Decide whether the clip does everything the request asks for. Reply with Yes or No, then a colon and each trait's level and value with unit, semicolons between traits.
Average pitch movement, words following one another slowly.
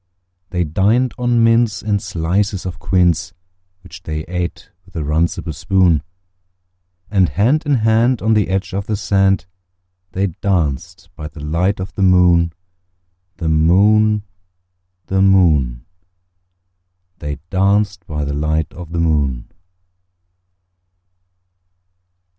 Yes: average, 3.9 semitones; slow, 120 wpm